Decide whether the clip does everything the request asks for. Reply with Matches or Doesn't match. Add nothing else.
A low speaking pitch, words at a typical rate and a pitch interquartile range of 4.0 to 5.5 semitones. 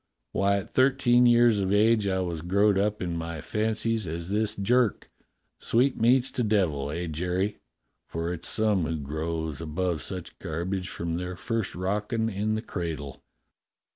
Matches